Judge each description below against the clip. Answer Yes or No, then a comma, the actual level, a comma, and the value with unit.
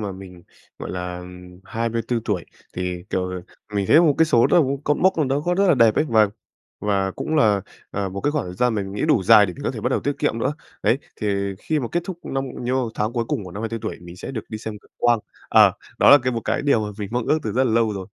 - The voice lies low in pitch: Yes, low, 110 Hz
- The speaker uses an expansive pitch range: No, average, 4.9 semitones